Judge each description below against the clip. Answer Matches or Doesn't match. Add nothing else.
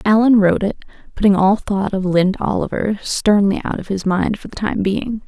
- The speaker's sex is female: Matches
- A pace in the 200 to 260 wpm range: Matches